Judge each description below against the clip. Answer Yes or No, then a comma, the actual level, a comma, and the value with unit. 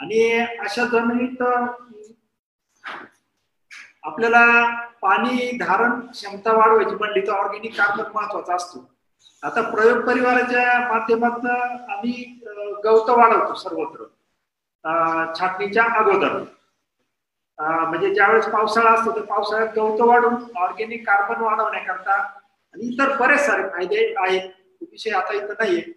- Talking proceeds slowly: Yes, slow, 105 wpm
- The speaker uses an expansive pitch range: No, average, 2.8 semitones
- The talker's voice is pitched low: No, high, 225 Hz